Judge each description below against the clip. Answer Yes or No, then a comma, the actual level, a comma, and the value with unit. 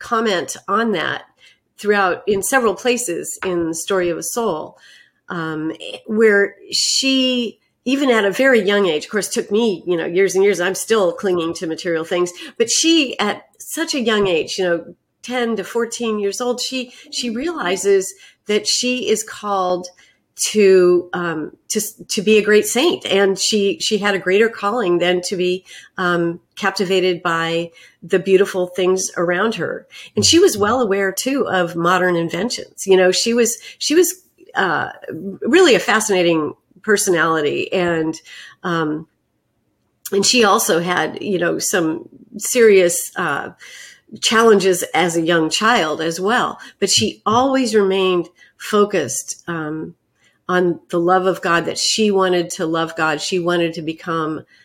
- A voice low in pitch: No, high, 195 Hz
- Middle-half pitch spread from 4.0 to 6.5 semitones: Yes, average, 5.0 semitones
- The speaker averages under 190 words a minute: Yes, average, 155 wpm